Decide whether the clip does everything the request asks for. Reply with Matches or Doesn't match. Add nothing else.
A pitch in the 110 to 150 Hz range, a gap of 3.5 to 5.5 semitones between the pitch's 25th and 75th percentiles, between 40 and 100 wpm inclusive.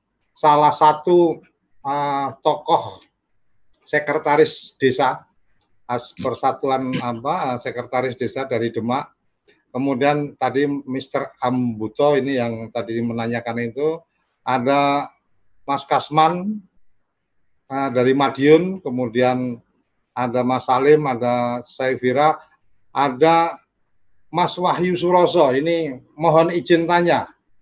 Matches